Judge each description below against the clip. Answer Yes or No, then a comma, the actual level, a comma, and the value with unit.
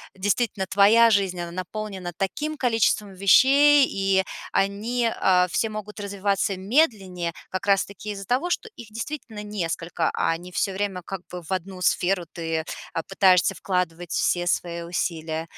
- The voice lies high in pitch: Yes, high, 195 Hz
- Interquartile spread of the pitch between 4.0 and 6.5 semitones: No, average, 3.1 semitones